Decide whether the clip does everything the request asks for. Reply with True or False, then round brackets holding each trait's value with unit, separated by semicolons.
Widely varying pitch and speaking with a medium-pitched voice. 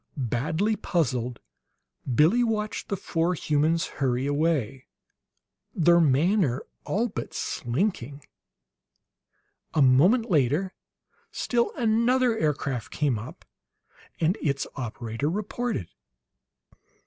True (7.8 semitones; 155 Hz)